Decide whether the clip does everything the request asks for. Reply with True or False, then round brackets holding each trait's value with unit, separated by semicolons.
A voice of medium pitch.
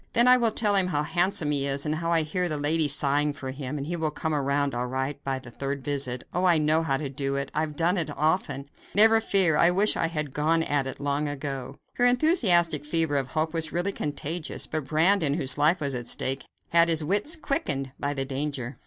True (150 Hz)